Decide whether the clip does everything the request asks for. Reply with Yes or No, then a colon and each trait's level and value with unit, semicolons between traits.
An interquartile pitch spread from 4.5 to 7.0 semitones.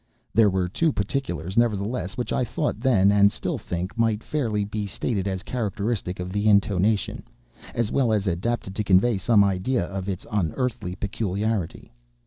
No: average, 3.3 semitones